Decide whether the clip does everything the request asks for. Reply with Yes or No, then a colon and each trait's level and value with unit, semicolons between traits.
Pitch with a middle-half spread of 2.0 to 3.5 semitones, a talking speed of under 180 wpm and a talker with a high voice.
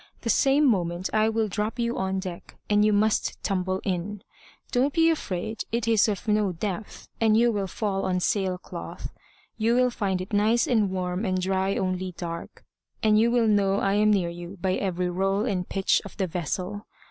No: average, 2.8 semitones; average, 195 wpm; high, 200 Hz